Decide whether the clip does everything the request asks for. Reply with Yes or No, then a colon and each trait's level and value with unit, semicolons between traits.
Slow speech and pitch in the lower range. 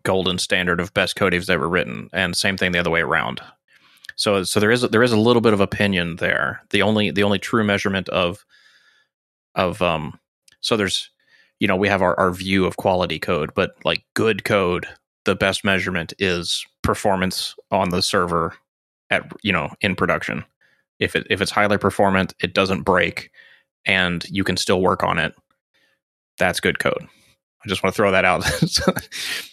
No: average, 185 wpm; very low, 95 Hz